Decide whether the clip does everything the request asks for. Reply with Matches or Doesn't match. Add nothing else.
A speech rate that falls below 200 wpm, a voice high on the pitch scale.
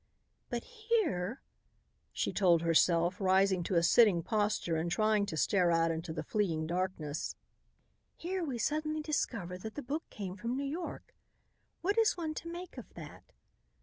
Matches